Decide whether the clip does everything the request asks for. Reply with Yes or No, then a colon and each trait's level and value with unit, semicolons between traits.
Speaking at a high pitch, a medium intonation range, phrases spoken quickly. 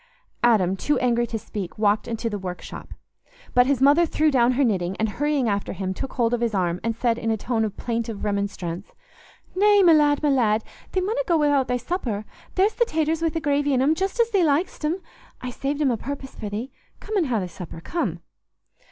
No: very high, 250 Hz; wide, 6.1 semitones; fast, 220 wpm